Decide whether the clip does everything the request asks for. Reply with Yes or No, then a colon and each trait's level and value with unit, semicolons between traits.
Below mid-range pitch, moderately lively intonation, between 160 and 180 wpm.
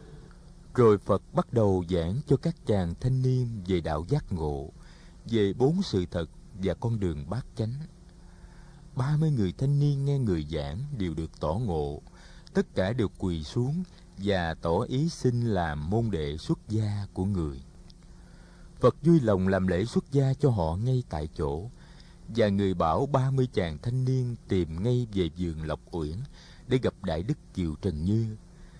No: low, 110 Hz; wide, 7.7 semitones; average, 175 wpm